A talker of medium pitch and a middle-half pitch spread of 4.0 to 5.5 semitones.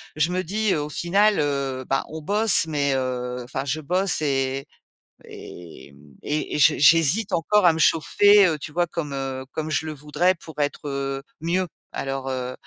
Yes: medium, 150 Hz; average, 4.4 semitones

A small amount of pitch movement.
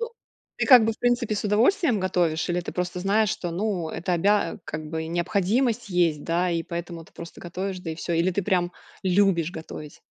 No: average, 3.6 semitones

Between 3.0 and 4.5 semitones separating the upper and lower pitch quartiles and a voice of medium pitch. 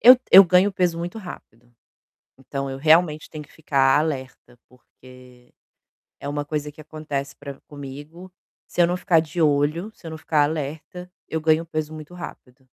Yes: average, 3.3 semitones; medium, 155 Hz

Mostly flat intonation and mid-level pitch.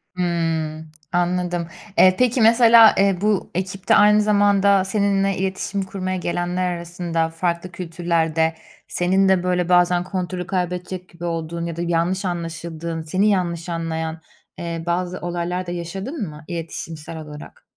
Yes: narrow, 2.1 semitones; medium, 175 Hz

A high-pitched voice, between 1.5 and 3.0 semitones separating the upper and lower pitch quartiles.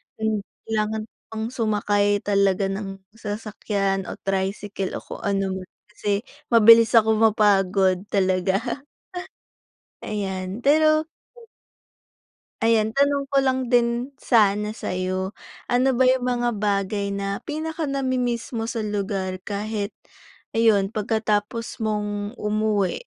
Yes: high, 210 Hz; average, 2.7 semitones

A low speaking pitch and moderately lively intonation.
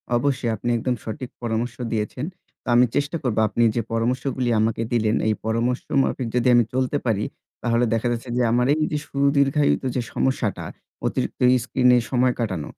No: low, 120 Hz; narrow, 2.2 semitones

